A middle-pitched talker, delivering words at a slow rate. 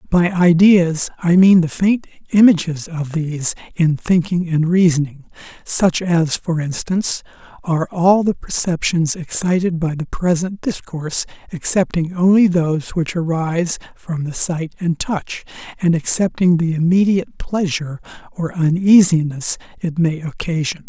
Yes: medium, 170 Hz; slow, 130 wpm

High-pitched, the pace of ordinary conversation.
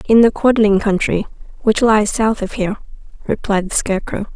Yes: high, 210 Hz; average, 165 wpm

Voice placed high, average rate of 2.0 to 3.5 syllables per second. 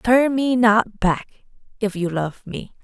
Yes: high, 215 Hz; 3.4 syllables/s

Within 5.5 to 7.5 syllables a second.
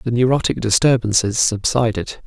No: 5.1 syllables/s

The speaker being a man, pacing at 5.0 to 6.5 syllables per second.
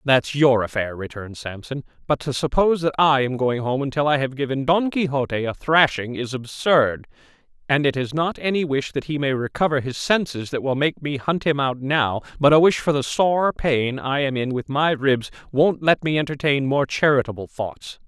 Yes: male; 5.1 syllables/s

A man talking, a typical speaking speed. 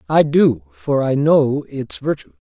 Yes: male; average, 170 wpm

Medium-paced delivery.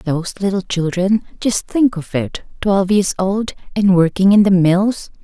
Yes: average, 150 wpm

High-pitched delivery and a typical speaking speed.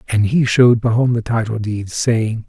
No: low, 115 Hz; average, 195 wpm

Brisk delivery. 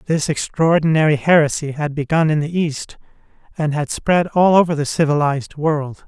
No: average, 160 wpm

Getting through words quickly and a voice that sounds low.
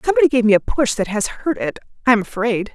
No: fast, 260 wpm; high, 235 Hz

